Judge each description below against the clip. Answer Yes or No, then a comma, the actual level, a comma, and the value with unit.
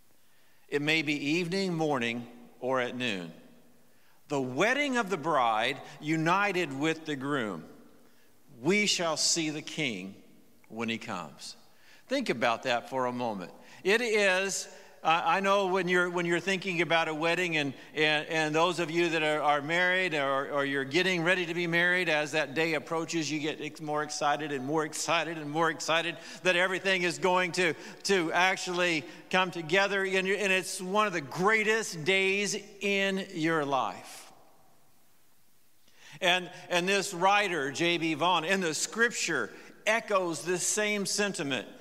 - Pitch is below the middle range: No, medium, 170 Hz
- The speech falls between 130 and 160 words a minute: Yes, average, 155 wpm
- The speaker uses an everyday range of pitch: Yes, average, 3.9 semitones